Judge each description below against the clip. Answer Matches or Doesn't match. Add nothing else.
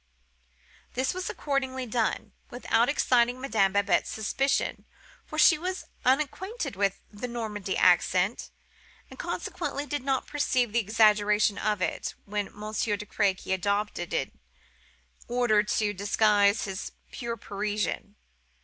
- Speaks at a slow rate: Matches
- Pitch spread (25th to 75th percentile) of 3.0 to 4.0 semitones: Matches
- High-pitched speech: Matches